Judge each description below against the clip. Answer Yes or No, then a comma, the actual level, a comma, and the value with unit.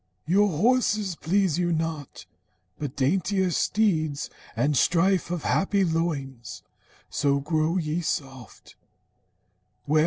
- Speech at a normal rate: No, slow, 100 wpm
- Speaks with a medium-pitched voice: Yes, medium, 165 Hz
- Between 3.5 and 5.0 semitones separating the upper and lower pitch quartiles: Yes, average, 4.3 semitones